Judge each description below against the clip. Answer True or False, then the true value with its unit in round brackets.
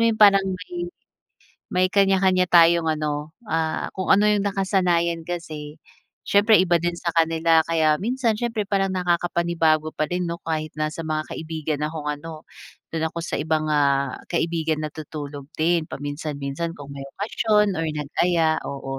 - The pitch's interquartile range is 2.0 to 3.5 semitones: True (3.1 semitones)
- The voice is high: False (165 Hz)